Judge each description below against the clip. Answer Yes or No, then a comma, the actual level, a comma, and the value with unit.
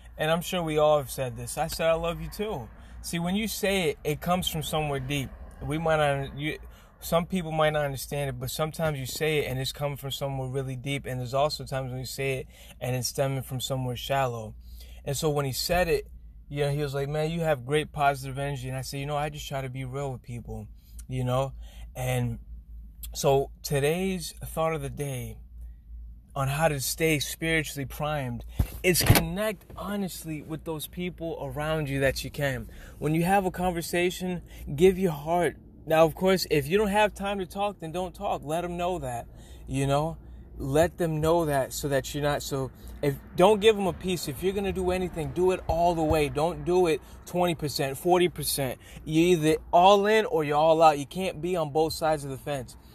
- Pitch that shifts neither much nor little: Yes, average, 4.1 semitones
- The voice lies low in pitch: No, medium, 150 Hz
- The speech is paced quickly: Yes, fast, 215 wpm